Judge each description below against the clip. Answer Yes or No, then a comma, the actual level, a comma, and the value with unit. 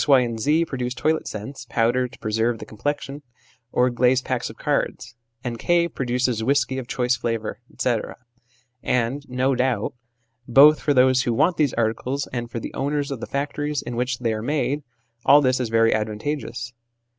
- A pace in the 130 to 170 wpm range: No, average, 180 wpm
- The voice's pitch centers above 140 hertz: No, low, 125 Hz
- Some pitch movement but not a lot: Yes, average, 3.0 semitones